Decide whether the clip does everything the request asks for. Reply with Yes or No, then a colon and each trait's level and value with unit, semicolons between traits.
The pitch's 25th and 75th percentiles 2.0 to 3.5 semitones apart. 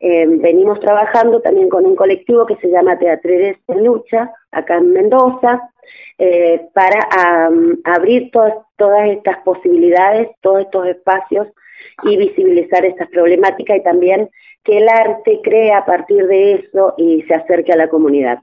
No: average, 4.2 semitones